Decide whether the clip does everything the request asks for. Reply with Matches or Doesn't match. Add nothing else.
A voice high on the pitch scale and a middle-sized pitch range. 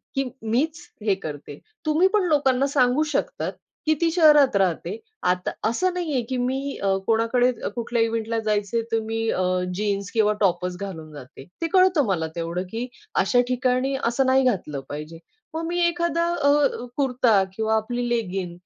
Doesn't match